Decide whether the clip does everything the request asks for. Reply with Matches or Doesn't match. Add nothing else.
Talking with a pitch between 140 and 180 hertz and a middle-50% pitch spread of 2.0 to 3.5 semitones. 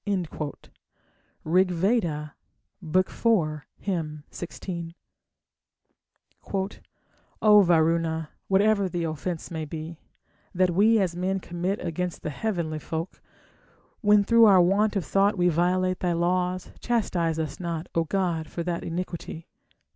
Matches